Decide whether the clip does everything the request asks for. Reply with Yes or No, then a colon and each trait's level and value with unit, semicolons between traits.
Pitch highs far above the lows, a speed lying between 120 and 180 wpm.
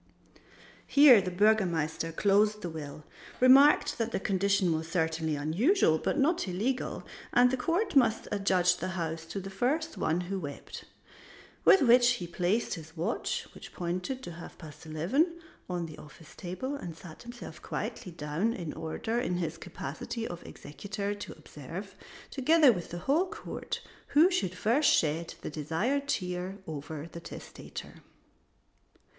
Yes: wide, 6.9 semitones; average, 150 wpm